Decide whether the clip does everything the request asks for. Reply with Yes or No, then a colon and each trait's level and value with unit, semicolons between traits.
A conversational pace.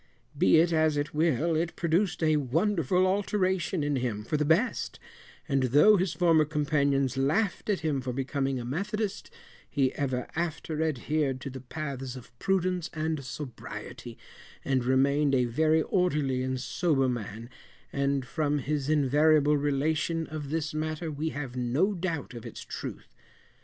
Yes: average, 155 wpm